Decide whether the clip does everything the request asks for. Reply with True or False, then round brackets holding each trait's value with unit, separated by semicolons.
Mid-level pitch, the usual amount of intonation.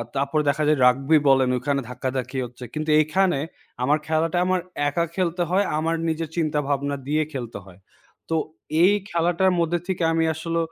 True (155 Hz; 3.5 semitones)